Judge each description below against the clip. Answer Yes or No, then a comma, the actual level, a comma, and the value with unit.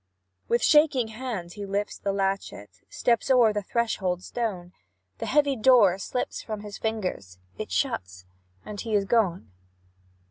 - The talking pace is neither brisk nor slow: Yes, average, 145 wpm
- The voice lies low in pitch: No, high, 205 Hz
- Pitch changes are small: No, average, 4.5 semitones